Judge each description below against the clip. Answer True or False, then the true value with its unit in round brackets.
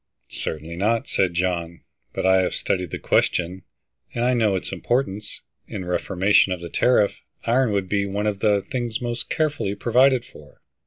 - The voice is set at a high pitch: False (100 Hz)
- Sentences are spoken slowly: False (175 wpm)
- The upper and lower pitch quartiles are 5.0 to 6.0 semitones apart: False (4.3 semitones)